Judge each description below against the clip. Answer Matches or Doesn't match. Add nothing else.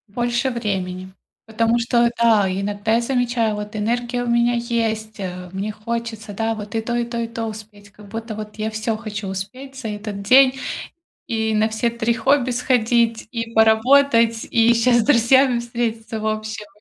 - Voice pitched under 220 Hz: Doesn't match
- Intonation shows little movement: Matches